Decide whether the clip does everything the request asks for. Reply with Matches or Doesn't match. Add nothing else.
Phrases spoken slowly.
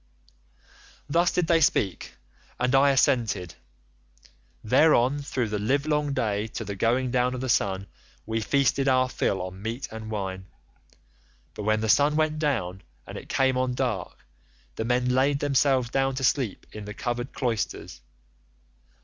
Doesn't match